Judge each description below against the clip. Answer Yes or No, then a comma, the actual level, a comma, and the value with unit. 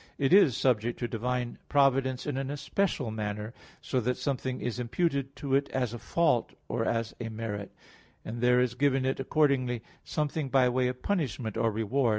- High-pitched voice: No, low, 125 Hz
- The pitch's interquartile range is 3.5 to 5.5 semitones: No, average, 2.8 semitones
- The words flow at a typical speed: Yes, average, 185 wpm